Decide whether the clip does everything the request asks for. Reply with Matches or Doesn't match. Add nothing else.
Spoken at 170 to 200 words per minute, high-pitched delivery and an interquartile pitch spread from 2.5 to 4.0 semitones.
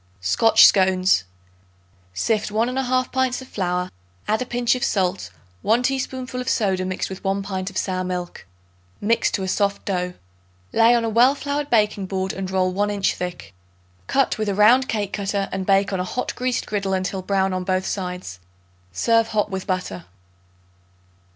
Matches